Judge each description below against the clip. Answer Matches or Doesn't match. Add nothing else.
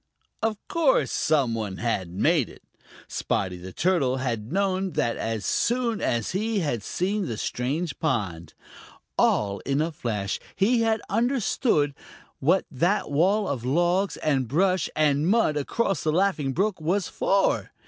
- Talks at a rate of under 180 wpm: Matches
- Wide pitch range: Matches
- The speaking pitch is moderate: Matches